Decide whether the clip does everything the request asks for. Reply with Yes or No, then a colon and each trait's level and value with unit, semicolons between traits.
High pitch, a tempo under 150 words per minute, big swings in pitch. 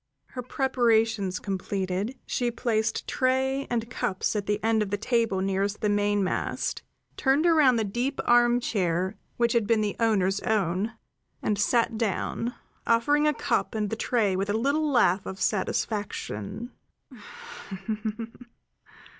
No: high, 220 Hz; slow, 135 wpm; average, 3.3 semitones